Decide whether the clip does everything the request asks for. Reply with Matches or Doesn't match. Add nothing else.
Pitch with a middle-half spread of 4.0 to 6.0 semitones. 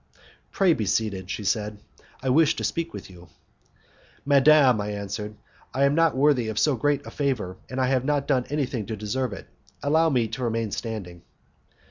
Matches